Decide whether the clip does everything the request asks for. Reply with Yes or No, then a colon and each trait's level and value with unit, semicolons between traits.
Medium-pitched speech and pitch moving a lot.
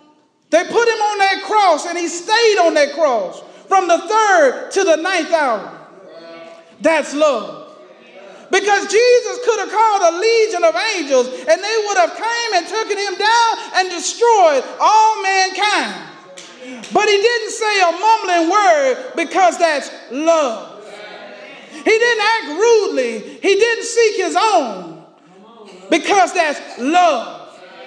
No: very high, 365 Hz; wide, 5.9 semitones